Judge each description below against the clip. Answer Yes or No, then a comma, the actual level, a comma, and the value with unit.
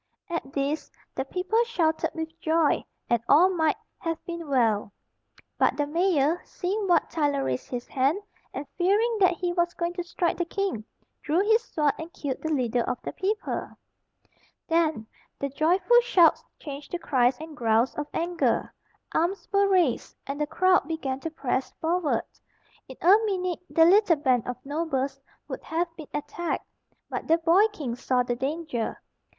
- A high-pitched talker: Yes, very high, 320 Hz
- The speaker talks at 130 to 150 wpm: No, average, 165 wpm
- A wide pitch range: No, average, 4.4 semitones